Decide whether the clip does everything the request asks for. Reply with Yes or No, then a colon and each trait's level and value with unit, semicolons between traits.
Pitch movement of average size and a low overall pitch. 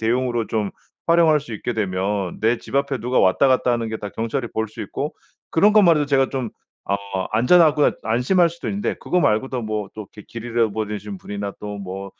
Yes: average, 4.8 semitones; low, 115 Hz